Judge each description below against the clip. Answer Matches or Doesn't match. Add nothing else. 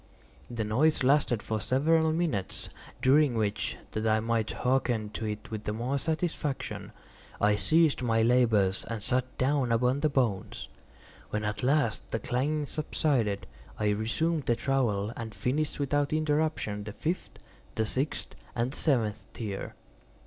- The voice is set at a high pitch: Doesn't match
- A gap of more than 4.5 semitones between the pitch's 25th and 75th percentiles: Matches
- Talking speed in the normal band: Matches